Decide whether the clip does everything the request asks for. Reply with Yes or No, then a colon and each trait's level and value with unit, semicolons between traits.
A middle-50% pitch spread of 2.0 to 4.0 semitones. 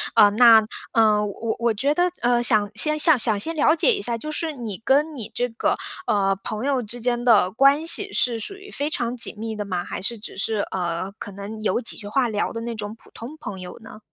No: average, 4.6 semitones